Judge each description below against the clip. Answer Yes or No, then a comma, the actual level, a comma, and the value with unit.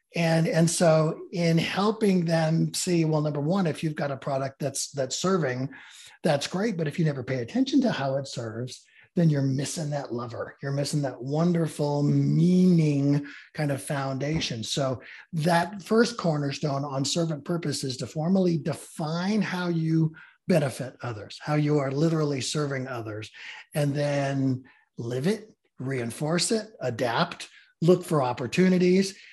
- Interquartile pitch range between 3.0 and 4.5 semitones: Yes, average, 4.0 semitones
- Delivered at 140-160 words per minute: Yes, average, 150 wpm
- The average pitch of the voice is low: No, medium, 155 Hz